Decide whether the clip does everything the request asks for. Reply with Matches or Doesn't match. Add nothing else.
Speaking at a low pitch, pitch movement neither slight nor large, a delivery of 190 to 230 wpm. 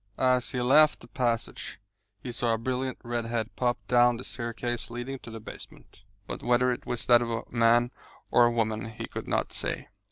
Doesn't match